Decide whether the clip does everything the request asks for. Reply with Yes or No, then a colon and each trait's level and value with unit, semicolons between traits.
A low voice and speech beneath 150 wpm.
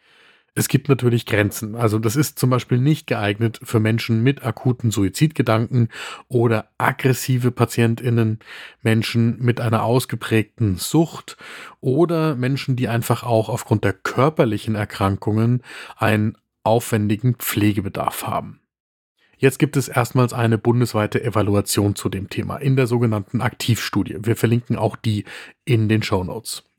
Yes: low, 115 Hz; average, 130 wpm